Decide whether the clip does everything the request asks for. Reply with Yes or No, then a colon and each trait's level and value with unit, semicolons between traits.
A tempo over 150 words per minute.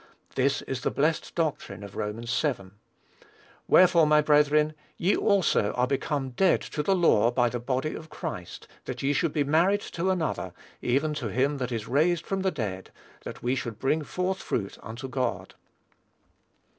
Yes: average, 170 wpm